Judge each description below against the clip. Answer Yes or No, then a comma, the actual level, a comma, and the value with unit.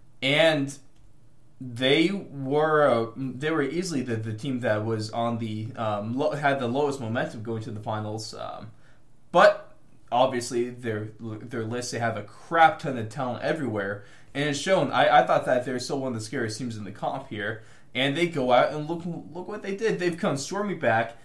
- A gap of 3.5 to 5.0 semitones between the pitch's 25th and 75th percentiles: Yes, average, 4.4 semitones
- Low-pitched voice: Yes, low, 125 Hz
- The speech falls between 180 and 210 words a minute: Yes, average, 200 wpm